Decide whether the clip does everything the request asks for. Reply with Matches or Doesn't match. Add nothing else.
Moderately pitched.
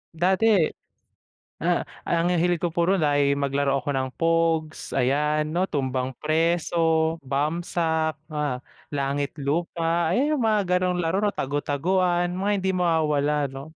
Matches